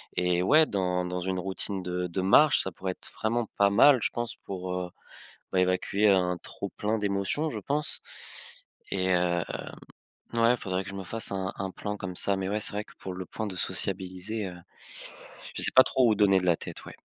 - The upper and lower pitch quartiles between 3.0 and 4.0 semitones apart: No, narrow, 2.5 semitones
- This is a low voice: Yes, very low, 95 Hz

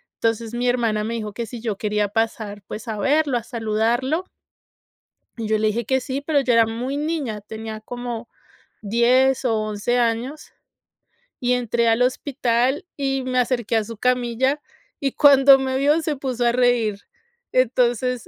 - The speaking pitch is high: Yes, high, 240 Hz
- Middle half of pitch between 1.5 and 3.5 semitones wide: Yes, average, 2.7 semitones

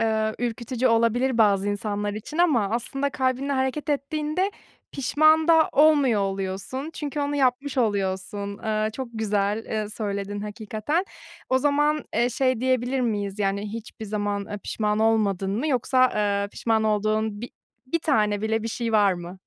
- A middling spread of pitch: Yes, average, 4.3 semitones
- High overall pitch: Yes, high, 225 Hz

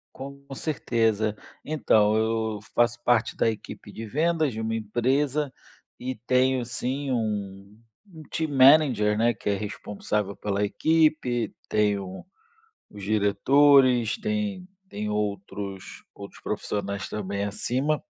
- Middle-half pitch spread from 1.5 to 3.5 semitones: No, average, 4.8 semitones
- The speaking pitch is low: Yes, low, 115 Hz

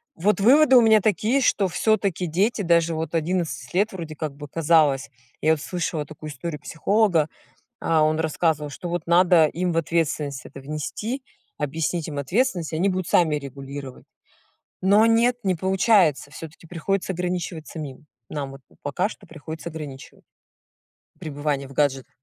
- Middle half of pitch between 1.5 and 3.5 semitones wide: No, average, 3.9 semitones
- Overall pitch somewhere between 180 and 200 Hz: No, medium, 165 Hz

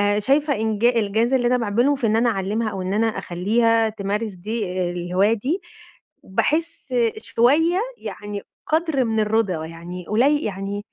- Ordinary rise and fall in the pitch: Yes, average, 3.6 semitones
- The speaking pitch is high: Yes, high, 220 Hz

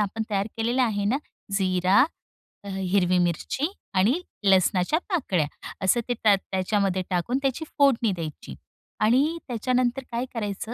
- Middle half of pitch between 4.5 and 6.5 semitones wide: Yes, average, 4.8 semitones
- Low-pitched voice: No, high, 205 Hz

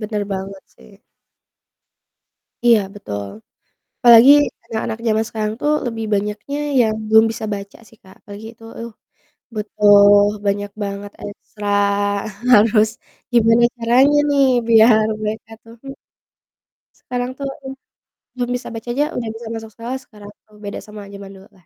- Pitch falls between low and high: No, high, 220 Hz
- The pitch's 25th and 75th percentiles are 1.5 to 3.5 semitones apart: Yes, average, 2.7 semitones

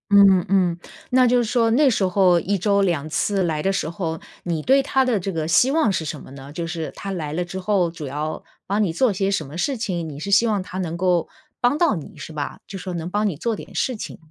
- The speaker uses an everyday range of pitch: Yes, average, 4.2 semitones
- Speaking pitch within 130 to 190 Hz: Yes, medium, 185 Hz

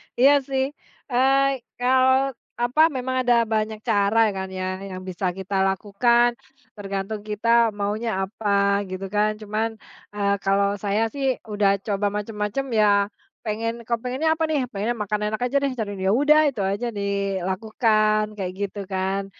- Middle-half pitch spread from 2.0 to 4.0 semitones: Yes, average, 3.3 semitones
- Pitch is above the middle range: Yes, high, 210 Hz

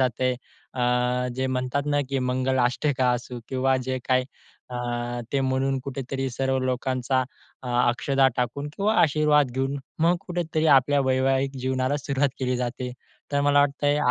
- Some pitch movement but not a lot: No, narrow, 1.8 semitones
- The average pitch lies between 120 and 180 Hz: Yes, low, 130 Hz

